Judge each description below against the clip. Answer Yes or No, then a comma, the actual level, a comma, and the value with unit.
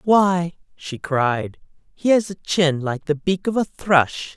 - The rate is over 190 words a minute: No, average, 180 wpm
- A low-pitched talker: No, medium, 170 Hz